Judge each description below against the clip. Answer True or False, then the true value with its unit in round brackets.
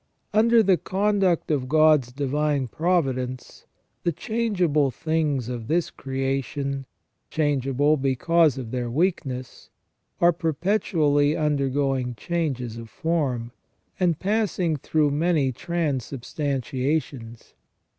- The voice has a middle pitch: True (145 Hz)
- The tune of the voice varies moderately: True (4.4 semitones)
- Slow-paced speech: True (95 wpm)